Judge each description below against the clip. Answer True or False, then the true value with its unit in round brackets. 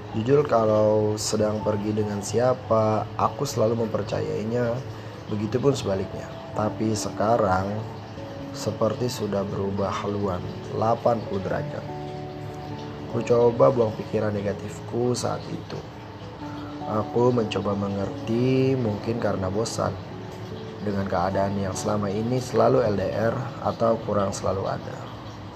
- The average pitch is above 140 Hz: False (110 Hz)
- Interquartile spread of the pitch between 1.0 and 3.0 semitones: True (2.6 semitones)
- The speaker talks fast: False (105 wpm)